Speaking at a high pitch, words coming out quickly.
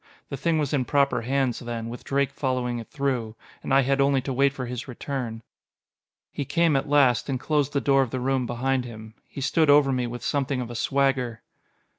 No: low, 135 Hz; fast, 215 wpm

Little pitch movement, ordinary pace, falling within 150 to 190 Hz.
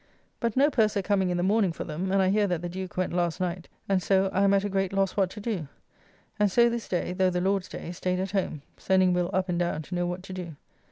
No: narrow, 1.8 semitones; fast, 275 wpm; medium, 185 Hz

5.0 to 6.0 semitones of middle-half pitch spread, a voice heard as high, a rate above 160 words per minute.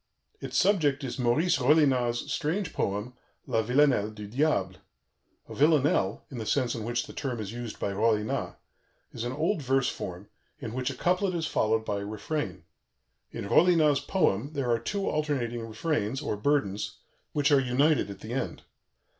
No: wide, 5.4 semitones; low, 125 Hz; average, 170 wpm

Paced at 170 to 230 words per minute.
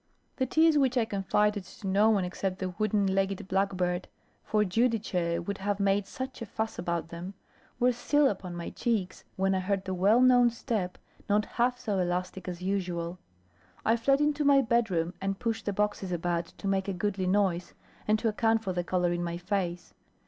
Yes: average, 190 wpm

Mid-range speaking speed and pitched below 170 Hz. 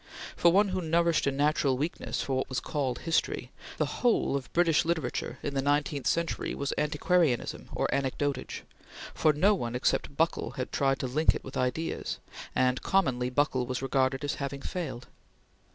Yes: average, 170 wpm; medium, 140 Hz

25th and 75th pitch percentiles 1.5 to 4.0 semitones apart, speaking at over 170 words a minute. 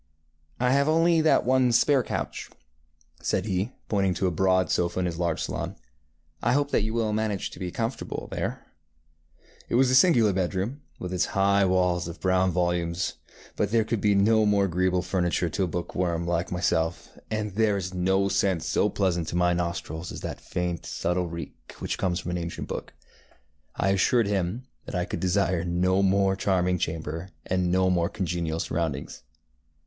Yes: average, 2.8 semitones; average, 180 wpm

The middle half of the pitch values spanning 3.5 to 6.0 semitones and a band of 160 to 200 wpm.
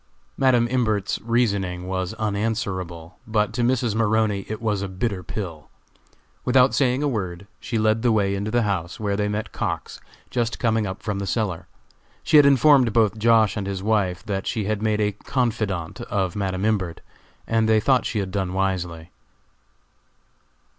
No: average, 3.0 semitones; average, 170 wpm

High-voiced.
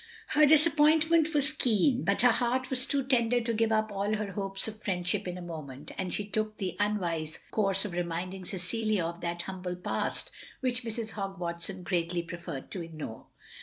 Yes: high, 200 Hz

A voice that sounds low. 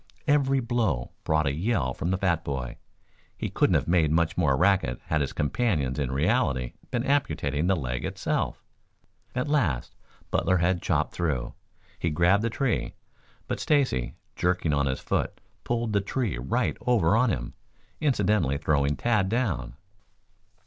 Yes: very low, 85 Hz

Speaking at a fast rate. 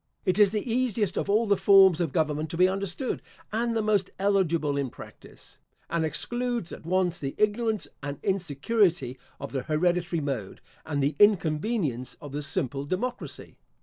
No: average, 165 wpm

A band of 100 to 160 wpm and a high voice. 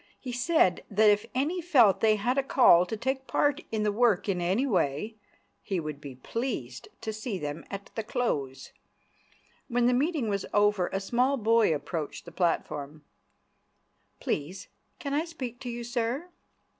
No: average, 170 wpm; high, 220 Hz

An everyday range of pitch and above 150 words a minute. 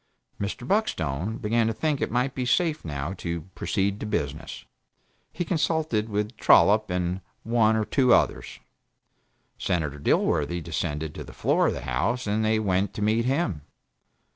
No: wide, 5.8 semitones; average, 160 wpm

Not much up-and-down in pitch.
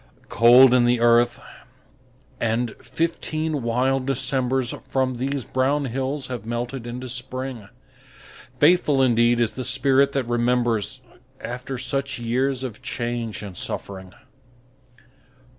Yes: narrow, 2.1 semitones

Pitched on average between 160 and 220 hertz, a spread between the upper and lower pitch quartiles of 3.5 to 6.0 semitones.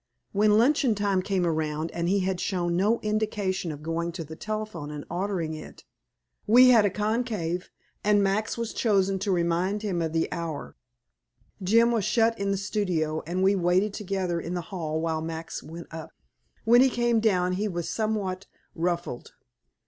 Yes: high, 190 Hz; average, 3.9 semitones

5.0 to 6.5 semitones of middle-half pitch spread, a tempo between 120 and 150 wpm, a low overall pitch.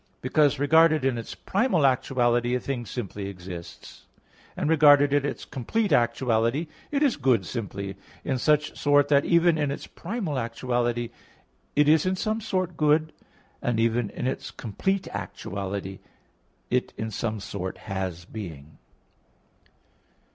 Yes: wide, 5.5 semitones; average, 140 wpm; low, 130 Hz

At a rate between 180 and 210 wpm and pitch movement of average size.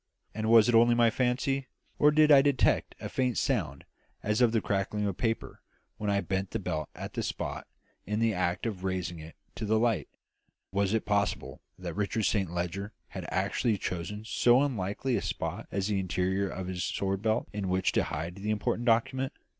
Yes: average, 195 wpm; average, 3.7 semitones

